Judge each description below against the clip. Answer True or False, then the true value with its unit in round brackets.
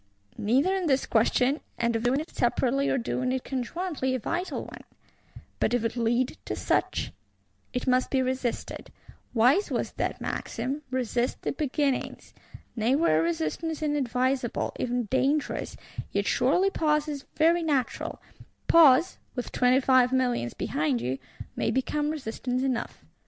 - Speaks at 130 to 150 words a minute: True (140 wpm)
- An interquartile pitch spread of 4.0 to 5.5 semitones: False (3.4 semitones)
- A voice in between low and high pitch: False (260 Hz)